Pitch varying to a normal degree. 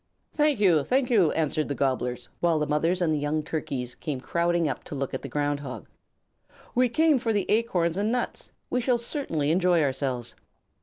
No: wide, 7.2 semitones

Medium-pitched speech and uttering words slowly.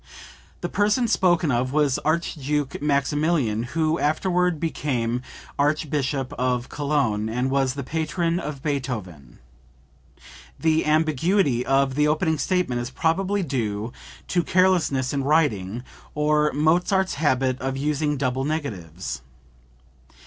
Yes: medium, 145 Hz; slow, 115 wpm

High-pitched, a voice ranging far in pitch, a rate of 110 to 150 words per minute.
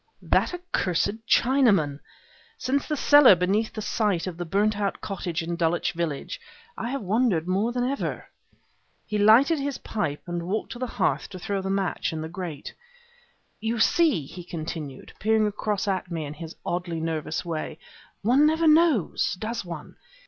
No: high, 195 Hz; wide, 5.7 semitones; average, 170 wpm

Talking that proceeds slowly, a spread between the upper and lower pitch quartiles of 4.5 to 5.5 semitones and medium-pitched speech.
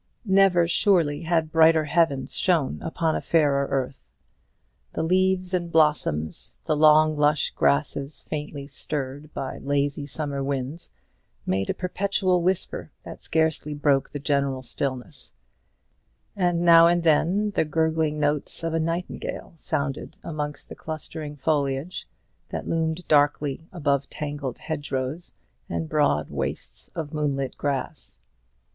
No: slow, 125 wpm; average, 3.0 semitones; medium, 150 Hz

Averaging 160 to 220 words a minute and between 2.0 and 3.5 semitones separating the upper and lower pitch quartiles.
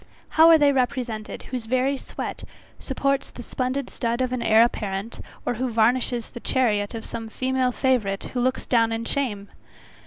Yes: average, 165 wpm; narrow, 2.5 semitones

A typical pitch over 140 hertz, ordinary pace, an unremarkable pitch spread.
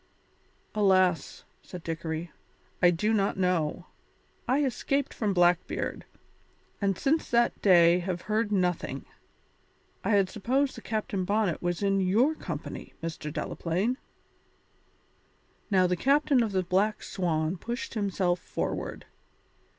No: high, 190 Hz; slow, 120 wpm; average, 3.9 semitones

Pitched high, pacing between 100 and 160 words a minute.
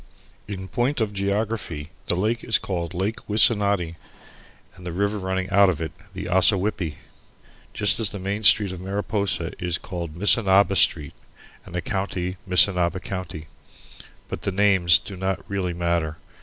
No: very low, 95 Hz; average, 155 wpm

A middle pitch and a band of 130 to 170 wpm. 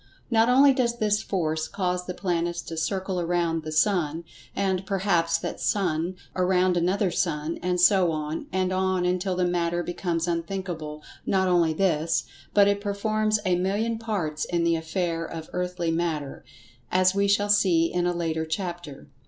Yes: medium, 180 Hz; average, 160 wpm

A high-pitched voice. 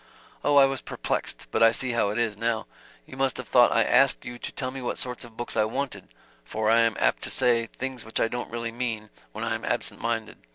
No: low, 115 Hz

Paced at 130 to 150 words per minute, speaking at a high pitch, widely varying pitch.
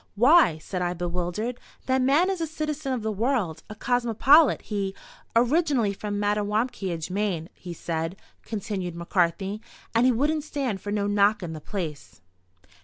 Yes: average, 145 wpm; high, 210 Hz; wide, 5.9 semitones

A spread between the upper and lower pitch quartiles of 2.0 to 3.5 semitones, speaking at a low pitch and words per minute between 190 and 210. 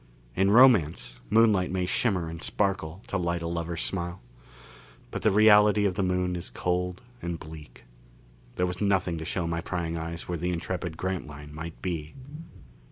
No: narrow, 2.4 semitones; very low, 90 Hz; average, 165 wpm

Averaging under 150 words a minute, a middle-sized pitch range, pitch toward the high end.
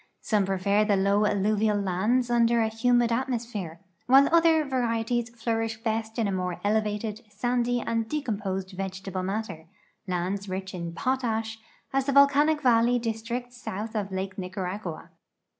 Yes: average, 140 wpm; average, 3.8 semitones; high, 220 Hz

